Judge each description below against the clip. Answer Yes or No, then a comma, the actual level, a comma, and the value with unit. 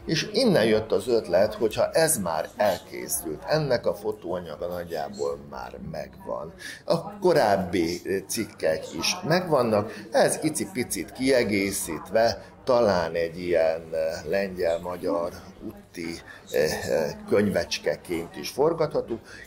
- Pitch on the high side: No, low, 105 Hz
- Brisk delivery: No, slow, 95 wpm